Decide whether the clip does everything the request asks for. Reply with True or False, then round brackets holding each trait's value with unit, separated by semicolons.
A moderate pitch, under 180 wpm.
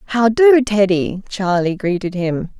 False (200 Hz; 140 wpm)